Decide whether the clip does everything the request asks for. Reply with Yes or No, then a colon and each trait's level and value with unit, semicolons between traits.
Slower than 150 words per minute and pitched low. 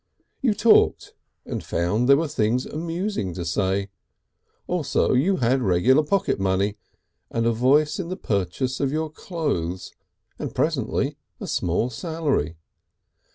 Yes: slow, 135 wpm; low, 130 Hz